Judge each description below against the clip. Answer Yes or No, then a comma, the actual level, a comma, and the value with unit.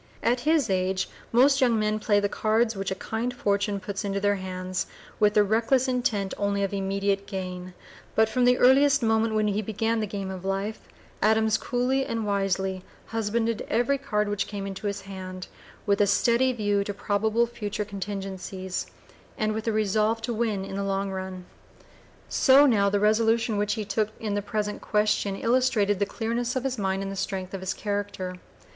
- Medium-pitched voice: No, high, 210 Hz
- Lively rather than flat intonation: No, narrow, 2.5 semitones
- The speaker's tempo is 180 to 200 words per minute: Yes, average, 190 wpm